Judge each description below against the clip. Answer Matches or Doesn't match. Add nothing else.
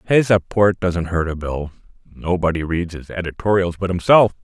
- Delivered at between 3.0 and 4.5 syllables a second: Doesn't match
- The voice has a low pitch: Matches